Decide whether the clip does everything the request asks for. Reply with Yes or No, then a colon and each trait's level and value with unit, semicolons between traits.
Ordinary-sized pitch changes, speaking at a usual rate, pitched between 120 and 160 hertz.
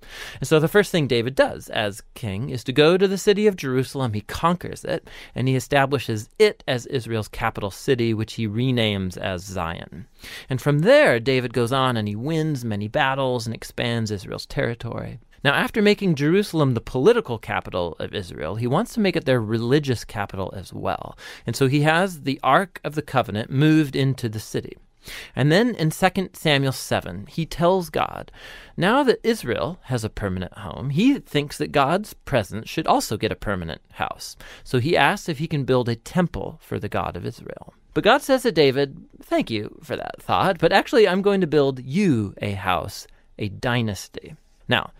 No: wide, 6.5 semitones; average, 190 wpm; low, 135 Hz